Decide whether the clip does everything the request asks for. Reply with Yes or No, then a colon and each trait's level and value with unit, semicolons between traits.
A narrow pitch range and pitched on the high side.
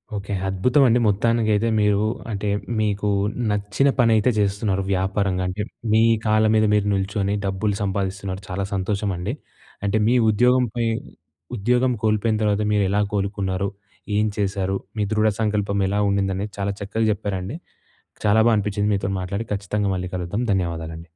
No: narrow, 1.8 semitones; low, 100 Hz